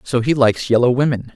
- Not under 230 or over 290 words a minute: No, fast, 220 wpm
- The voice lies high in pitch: No, low, 125 Hz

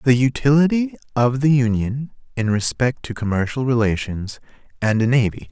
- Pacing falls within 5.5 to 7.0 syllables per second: No, 5.0 syllables/s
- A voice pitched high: No, low, 125 Hz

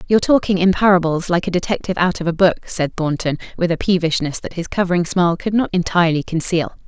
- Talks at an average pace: No, fast, 210 wpm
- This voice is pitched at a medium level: Yes, medium, 175 Hz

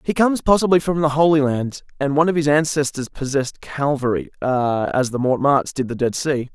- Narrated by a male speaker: Yes, male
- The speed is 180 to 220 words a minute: Yes, average, 190 wpm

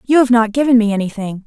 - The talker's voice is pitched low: No, high, 230 Hz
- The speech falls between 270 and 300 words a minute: No, fast, 245 wpm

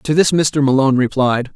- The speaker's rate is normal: Yes, average, 190 wpm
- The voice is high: No, medium, 140 Hz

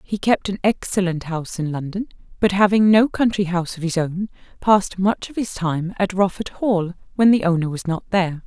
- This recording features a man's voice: No, female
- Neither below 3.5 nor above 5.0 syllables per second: No, 5.3 syllables/s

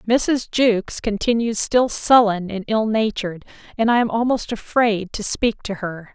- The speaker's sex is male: No, female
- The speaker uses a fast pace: No, average, 165 wpm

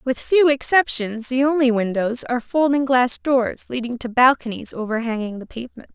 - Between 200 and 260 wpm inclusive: No, average, 160 wpm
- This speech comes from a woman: Yes, female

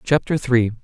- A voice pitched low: Yes, low, 120 Hz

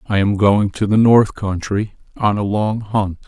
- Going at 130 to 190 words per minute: No, average, 200 wpm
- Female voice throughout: No, male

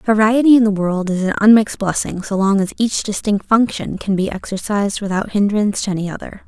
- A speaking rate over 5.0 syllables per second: Yes, 5.9 syllables/s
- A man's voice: No, female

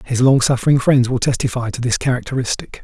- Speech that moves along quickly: No, average, 190 wpm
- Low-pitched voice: Yes, low, 125 Hz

